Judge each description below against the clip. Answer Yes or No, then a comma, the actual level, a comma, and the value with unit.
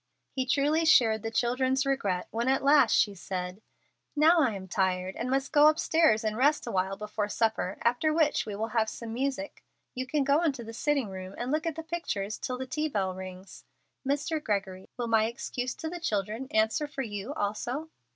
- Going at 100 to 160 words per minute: No, average, 200 wpm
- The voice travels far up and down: Yes, wide, 5.8 semitones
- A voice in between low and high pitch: No, high, 240 Hz